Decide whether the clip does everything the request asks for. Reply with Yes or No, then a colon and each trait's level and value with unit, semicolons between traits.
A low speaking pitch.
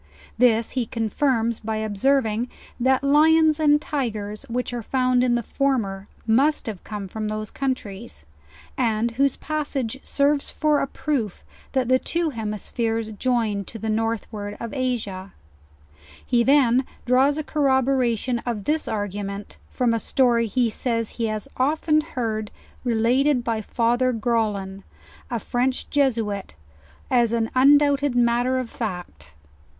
No: high, 235 Hz